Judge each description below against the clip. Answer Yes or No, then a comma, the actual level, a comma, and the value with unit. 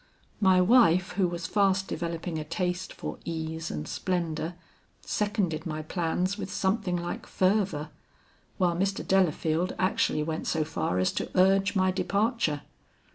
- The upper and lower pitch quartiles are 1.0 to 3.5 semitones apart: Yes, average, 3.0 semitones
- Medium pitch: Yes, medium, 180 Hz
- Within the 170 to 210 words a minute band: No, average, 140 wpm